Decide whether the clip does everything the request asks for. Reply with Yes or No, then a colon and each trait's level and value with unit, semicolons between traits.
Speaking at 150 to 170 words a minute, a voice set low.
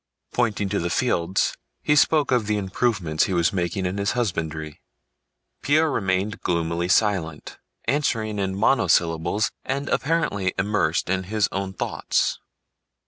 No: slow, 135 wpm; low, 100 Hz